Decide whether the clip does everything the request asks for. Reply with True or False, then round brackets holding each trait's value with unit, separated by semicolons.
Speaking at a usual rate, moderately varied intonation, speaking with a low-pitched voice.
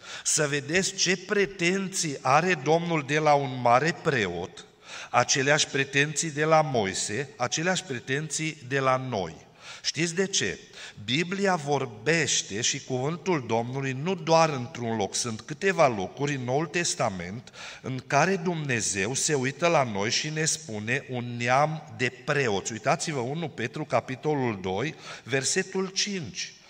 False (135 wpm; 4.5 semitones; 145 Hz)